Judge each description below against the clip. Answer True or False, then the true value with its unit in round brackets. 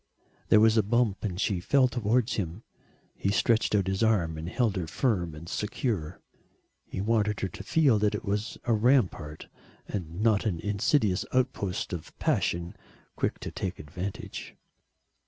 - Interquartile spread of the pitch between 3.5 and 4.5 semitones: True (4.0 semitones)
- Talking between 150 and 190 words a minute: True (160 wpm)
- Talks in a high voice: False (105 Hz)